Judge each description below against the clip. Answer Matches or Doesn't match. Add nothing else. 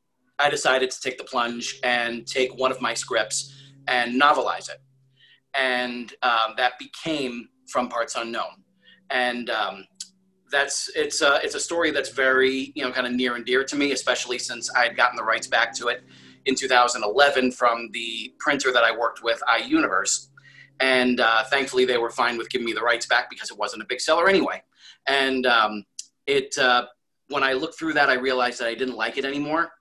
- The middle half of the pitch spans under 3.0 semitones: Matches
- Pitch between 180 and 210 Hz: Doesn't match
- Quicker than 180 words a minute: Matches